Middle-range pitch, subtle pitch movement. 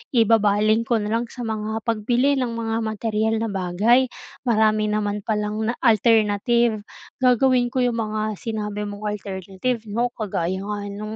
No: high, 215 Hz; narrow, 1.9 semitones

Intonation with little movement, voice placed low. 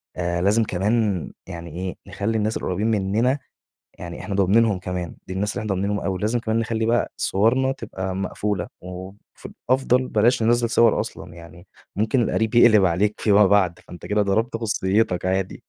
No: average, 3.4 semitones; low, 105 Hz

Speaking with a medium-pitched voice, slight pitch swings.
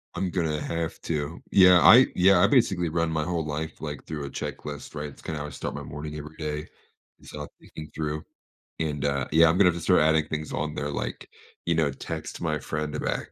No: very low, 75 Hz; narrow, 2.0 semitones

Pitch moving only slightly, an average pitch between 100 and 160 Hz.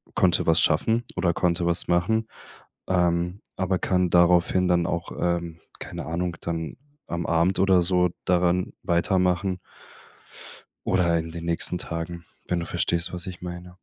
No: narrow, 1.2 semitones; very low, 85 Hz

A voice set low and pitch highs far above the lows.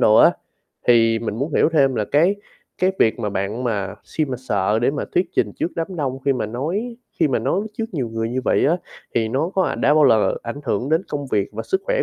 Yes: low, 130 Hz; wide, 6.2 semitones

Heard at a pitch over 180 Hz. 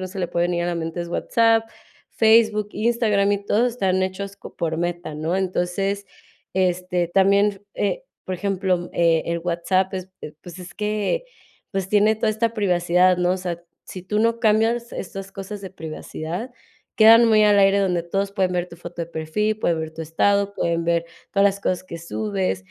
Yes: high, 190 Hz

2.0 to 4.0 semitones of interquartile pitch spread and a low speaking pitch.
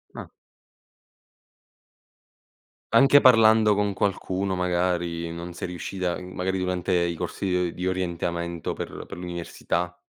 No: narrow, 1.6 semitones; very low, 90 Hz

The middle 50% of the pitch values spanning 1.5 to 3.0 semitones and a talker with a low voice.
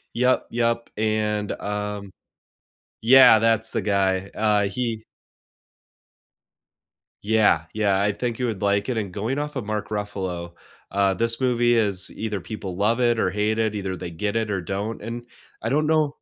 Yes: narrow, 2.5 semitones; low, 105 Hz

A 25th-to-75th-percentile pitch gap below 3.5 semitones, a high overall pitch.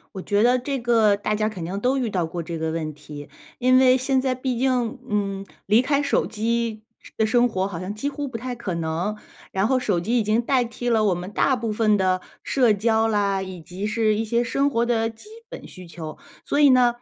No: average, 4.2 semitones; high, 220 Hz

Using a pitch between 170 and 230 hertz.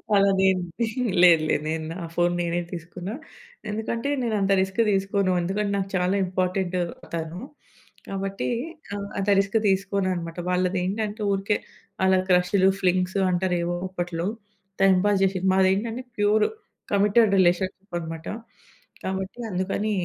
Yes: high, 190 Hz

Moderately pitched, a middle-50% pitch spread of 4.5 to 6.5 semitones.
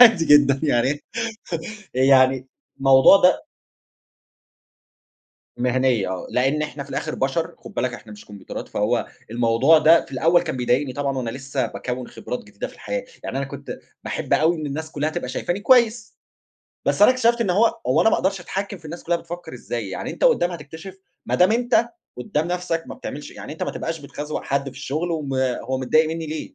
Yes: medium, 150 Hz; average, 5.0 semitones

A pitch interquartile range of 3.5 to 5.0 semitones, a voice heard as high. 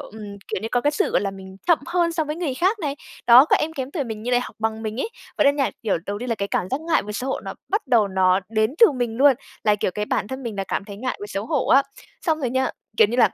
No: wide, 5.4 semitones; high, 245 Hz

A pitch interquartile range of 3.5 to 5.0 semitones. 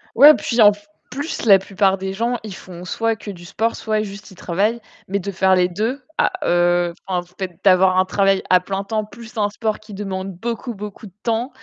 No: average, 2.9 semitones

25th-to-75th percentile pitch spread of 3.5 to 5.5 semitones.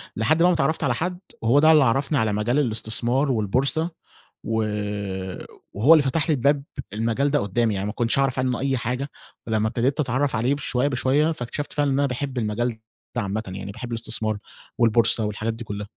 Yes: average, 4.1 semitones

